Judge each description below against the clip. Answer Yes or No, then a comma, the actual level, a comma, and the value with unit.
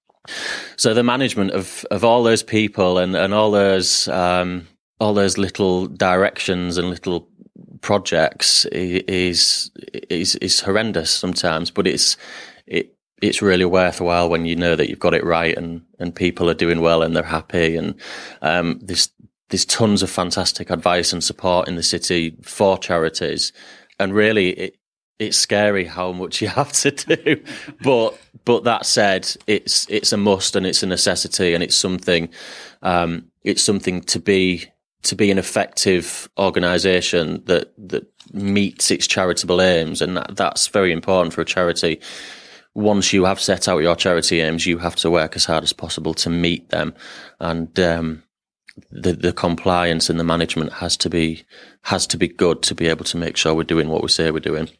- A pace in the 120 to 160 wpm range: No, average, 175 wpm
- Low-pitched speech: Yes, very low, 90 Hz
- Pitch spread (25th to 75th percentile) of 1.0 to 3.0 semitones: Yes, narrow, 2.4 semitones